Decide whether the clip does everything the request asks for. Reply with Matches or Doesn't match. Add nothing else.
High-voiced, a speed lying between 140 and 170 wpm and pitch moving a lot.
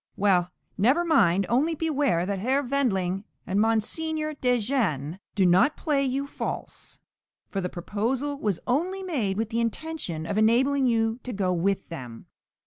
Matches